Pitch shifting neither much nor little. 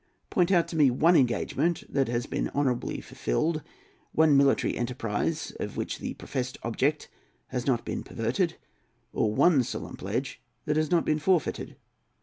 Yes: average, 4.6 semitones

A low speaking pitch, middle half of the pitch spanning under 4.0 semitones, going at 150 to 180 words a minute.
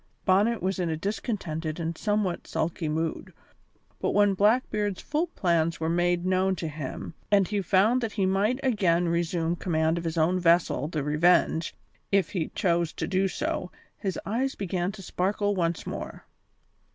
No: medium, 180 Hz; average, 3.3 semitones; average, 165 wpm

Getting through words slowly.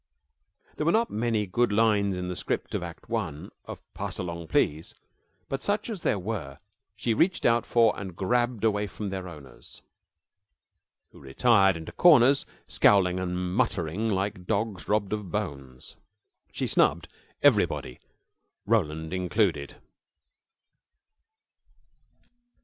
Yes: slow, 125 wpm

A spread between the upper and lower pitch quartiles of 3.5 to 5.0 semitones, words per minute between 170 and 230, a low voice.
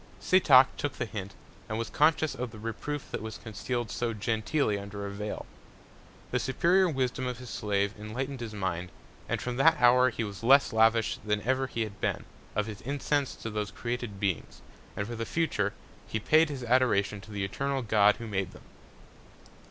Yes: average, 3.8 semitones; average, 185 wpm; low, 115 Hz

